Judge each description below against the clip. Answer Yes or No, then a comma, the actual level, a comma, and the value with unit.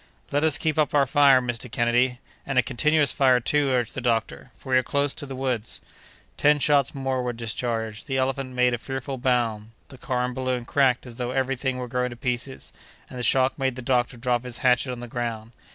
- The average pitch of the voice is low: Yes, low, 125 Hz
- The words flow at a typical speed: No, fast, 225 wpm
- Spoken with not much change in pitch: Yes, narrow, 1.8 semitones